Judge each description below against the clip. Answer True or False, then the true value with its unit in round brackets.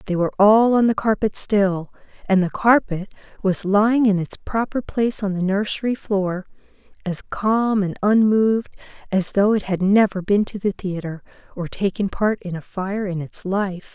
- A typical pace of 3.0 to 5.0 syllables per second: True (4.7 syllables/s)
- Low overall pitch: False (200 Hz)